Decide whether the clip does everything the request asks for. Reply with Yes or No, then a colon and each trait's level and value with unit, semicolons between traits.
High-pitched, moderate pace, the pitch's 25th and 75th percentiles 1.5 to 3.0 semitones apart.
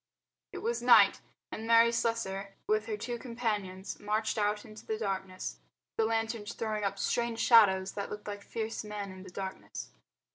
Yes: high, 215 Hz; average, 170 wpm; narrow, 2.4 semitones